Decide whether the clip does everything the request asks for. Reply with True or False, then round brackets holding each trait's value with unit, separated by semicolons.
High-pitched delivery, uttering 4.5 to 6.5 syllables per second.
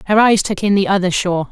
False (195 Hz; 6.9 syllables/s)